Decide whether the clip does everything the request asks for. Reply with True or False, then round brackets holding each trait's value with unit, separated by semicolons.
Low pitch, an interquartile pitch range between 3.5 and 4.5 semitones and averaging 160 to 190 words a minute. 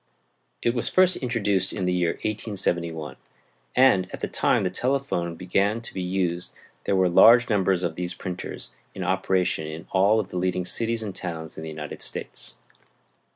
True (95 Hz; 3.8 semitones; 175 wpm)